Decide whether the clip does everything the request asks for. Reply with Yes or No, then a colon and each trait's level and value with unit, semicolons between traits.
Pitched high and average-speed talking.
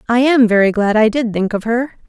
No: high, 230 Hz; fast, 260 wpm